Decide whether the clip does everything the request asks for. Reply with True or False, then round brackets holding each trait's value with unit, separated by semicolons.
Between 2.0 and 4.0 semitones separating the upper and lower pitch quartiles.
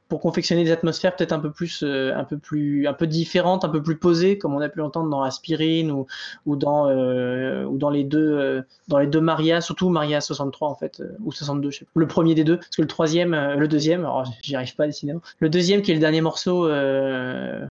True (2.7 semitones)